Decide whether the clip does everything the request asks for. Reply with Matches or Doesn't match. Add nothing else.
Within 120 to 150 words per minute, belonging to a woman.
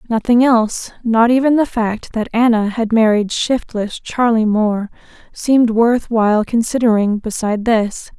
Matches